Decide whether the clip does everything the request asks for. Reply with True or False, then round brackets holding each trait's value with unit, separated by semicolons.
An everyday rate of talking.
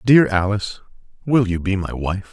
True (180 wpm)